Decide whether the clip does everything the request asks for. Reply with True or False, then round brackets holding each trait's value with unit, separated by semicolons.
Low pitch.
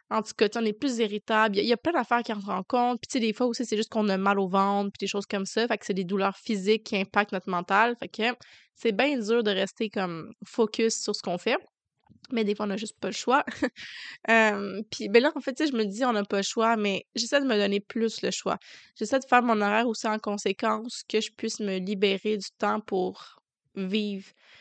False (215 Hz)